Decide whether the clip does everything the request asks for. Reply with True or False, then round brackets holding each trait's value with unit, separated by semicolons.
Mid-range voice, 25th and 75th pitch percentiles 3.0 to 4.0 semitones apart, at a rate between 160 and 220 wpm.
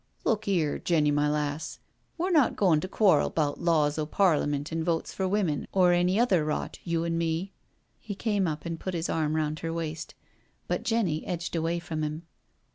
True (165 Hz; 3.4 semitones; 200 wpm)